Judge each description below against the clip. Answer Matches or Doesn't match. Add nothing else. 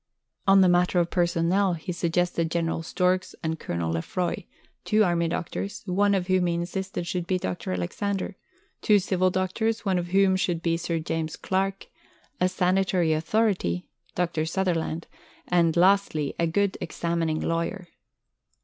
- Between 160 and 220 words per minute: Doesn't match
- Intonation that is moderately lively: Doesn't match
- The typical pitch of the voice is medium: Matches